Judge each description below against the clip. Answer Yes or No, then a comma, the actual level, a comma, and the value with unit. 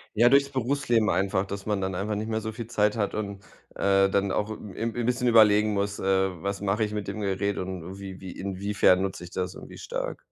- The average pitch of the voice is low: Yes, low, 100 Hz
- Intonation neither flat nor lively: No, narrow, 2.2 semitones